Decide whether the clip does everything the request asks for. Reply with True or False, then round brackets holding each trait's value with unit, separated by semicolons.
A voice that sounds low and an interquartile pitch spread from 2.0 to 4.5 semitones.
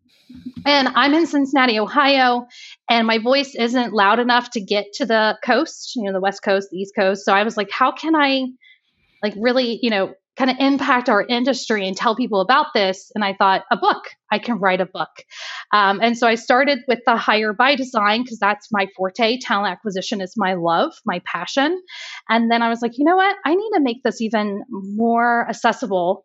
False (235 Hz; 4.0 semitones)